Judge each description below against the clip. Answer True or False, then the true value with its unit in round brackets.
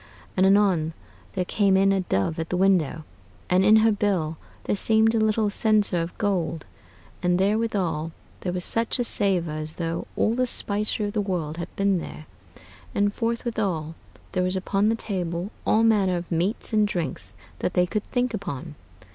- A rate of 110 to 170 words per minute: False (180 wpm)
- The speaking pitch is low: False (195 Hz)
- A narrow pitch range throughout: False (3.8 semitones)